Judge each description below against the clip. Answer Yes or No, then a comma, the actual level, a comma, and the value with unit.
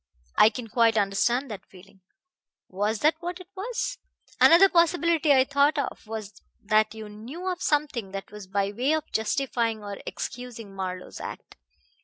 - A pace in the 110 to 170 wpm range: Yes, average, 160 wpm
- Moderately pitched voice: No, high, 230 Hz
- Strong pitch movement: Yes, wide, 6.7 semitones